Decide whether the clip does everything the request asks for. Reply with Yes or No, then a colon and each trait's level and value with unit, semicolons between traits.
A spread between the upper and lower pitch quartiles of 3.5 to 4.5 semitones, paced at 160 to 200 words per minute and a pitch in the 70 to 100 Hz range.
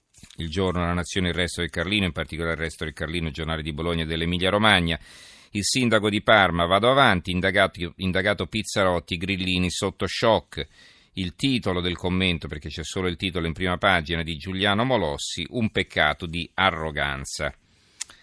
No: average, 2.7 semitones; fast, 170 wpm; very low, 90 Hz